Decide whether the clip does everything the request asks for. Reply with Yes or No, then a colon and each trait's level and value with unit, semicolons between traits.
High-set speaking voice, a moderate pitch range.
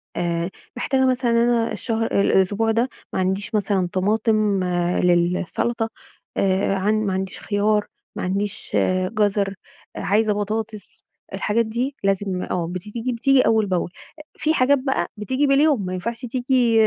Yes: high, 215 Hz; average, 3.6 semitones